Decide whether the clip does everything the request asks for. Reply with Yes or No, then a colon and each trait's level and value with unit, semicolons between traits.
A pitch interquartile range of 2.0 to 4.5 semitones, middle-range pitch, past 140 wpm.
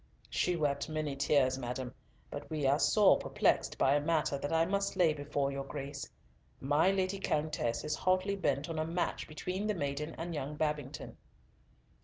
Yes: average, 3.2 semitones; medium, 150 Hz; average, 175 wpm